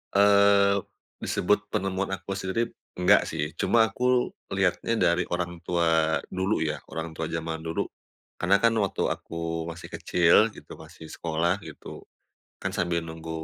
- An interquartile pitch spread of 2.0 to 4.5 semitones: Yes, average, 3.4 semitones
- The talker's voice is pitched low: Yes, very low, 90 Hz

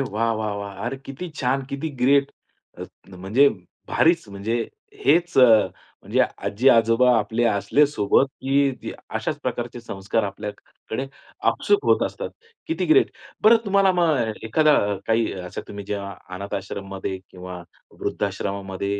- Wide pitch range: Yes, wide, 5.7 semitones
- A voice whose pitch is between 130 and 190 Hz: No, low, 115 Hz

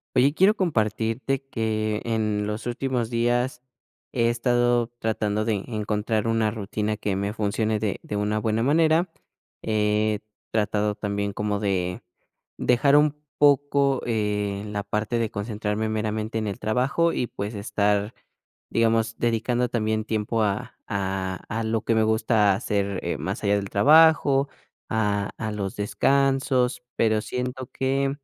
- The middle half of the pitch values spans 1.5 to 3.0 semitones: Yes, average, 2.7 semitones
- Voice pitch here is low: Yes, low, 110 Hz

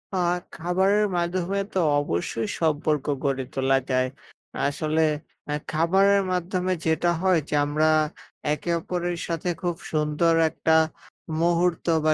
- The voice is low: No, medium, 165 Hz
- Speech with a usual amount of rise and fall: Yes, average, 3.0 semitones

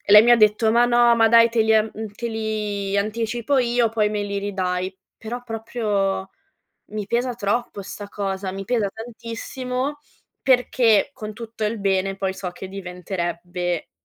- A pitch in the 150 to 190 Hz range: No, high, 215 Hz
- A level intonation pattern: No, average, 3.0 semitones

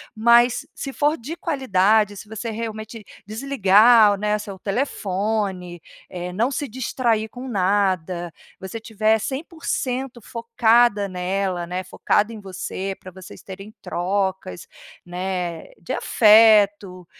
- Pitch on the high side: Yes, high, 210 Hz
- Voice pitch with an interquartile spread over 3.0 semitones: Yes, average, 3.6 semitones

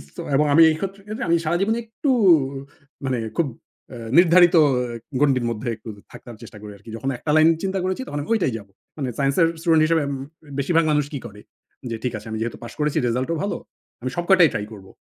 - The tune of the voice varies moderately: No, wide, 6.4 semitones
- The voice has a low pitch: No, medium, 150 Hz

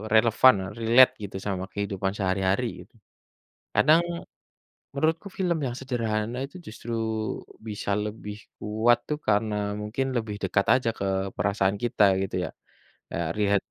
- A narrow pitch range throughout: No, average, 3.2 semitones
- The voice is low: Yes, low, 110 Hz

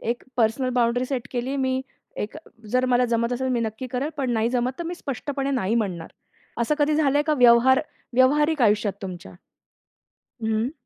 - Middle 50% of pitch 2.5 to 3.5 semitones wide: Yes, average, 2.8 semitones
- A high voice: Yes, very high, 250 Hz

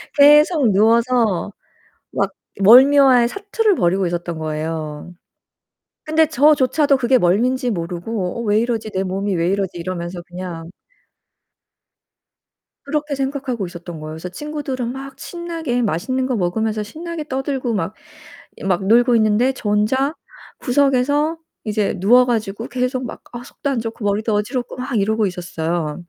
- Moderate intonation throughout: No, wide, 6.1 semitones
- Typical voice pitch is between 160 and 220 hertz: No, high, 230 Hz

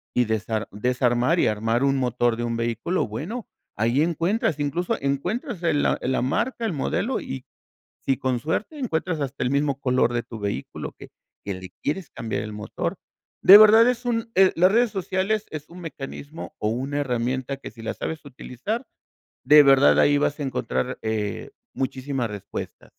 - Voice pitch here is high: No, medium, 140 Hz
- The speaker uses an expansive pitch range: Yes, wide, 6.8 semitones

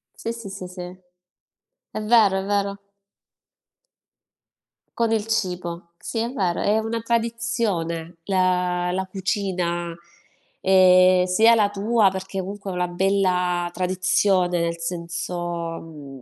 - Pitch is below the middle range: No, medium, 185 Hz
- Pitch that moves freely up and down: No, narrow, 2.6 semitones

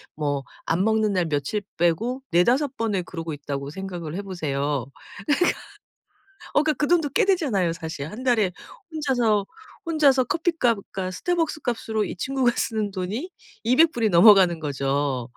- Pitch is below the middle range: No, high, 200 Hz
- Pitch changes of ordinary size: No, wide, 7.5 semitones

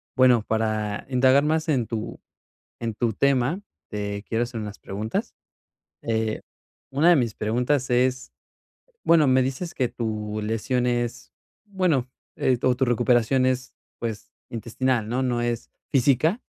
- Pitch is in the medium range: No, low, 125 Hz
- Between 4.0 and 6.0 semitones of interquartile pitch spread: No, average, 2.8 semitones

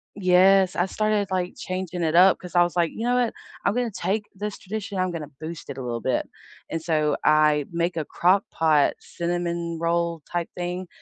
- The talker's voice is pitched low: No, medium, 175 Hz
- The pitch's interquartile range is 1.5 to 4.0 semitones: Yes, narrow, 2.6 semitones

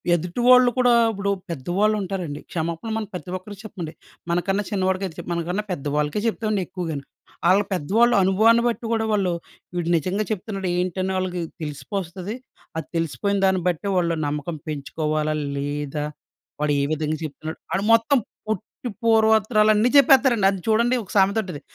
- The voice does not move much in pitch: No, average, 4.9 semitones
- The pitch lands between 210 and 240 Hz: No, high, 190 Hz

